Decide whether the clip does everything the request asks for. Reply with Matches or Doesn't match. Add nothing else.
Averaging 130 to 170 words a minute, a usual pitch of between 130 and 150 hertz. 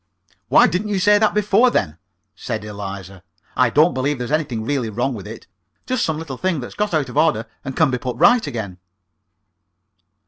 Doesn't match